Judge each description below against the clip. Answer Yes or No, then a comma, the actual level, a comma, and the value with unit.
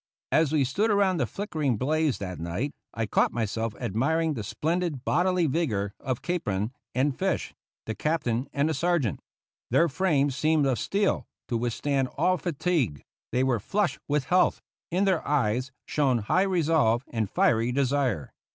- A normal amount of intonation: No, wide, 6.1 semitones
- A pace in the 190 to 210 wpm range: No, average, 160 wpm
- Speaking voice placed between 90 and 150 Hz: Yes, medium, 140 Hz